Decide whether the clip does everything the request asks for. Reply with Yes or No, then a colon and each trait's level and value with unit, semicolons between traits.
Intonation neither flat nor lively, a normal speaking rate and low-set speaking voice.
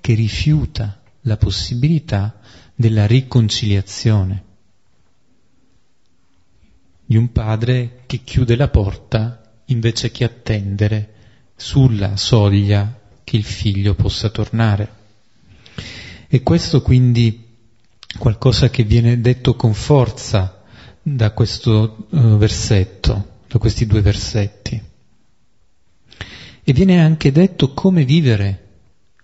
No: average, 3.2 semitones; slow, 90 wpm; low, 110 Hz